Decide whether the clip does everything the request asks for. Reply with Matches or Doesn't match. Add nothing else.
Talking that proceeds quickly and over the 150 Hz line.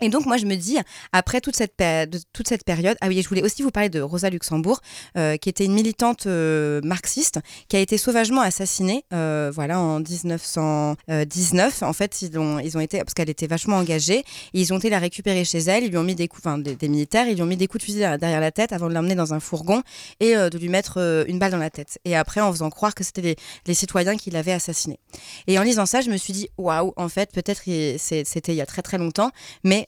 Matches